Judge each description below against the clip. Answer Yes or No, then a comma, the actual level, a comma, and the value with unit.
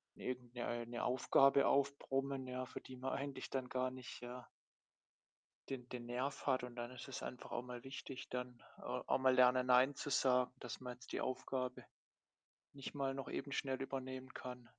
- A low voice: Yes, low, 130 Hz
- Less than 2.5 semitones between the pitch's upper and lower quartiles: Yes, narrow, 1.3 semitones